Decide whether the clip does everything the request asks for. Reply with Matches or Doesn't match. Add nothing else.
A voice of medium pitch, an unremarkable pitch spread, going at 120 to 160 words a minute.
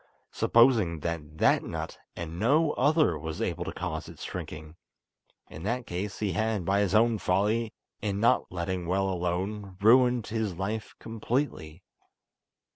Doesn't match